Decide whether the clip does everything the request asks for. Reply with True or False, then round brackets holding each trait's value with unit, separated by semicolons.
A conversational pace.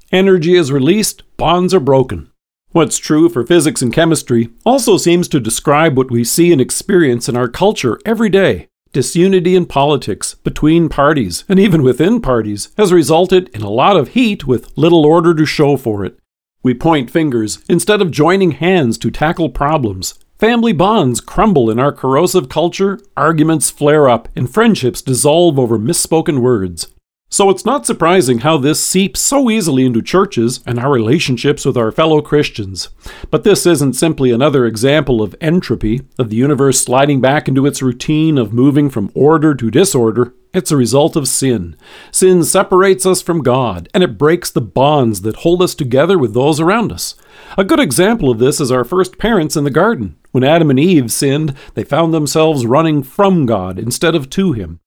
True (180 wpm)